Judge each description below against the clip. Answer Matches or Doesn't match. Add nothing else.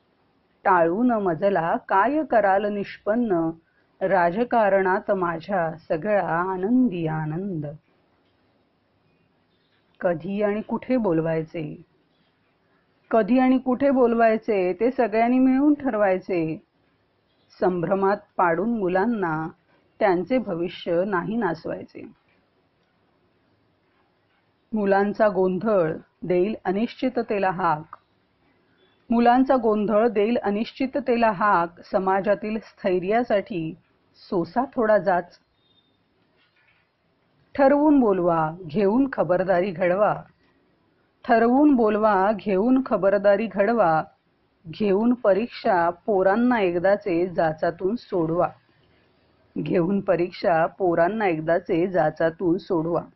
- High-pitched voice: Matches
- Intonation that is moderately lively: Matches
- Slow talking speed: Matches